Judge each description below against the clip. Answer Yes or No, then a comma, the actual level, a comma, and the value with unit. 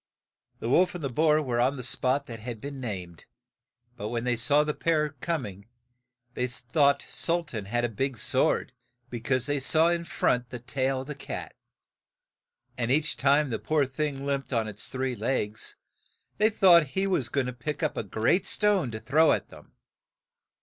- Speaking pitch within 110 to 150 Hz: Yes, low, 135 Hz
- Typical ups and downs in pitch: Yes, average, 4.1 semitones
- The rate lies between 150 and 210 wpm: Yes, average, 190 wpm